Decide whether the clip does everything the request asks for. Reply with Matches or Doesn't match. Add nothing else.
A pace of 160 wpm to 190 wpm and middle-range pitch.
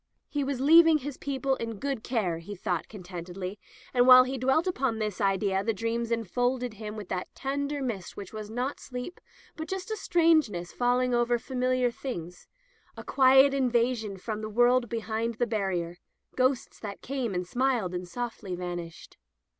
Doesn't match